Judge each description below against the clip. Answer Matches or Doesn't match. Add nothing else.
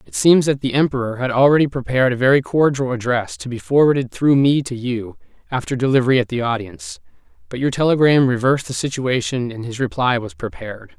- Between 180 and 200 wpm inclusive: Matches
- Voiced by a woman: Doesn't match